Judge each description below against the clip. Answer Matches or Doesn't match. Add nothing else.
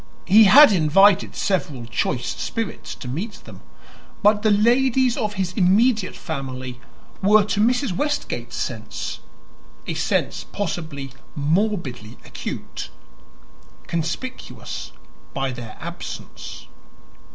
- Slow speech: Matches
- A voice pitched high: Matches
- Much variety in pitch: Matches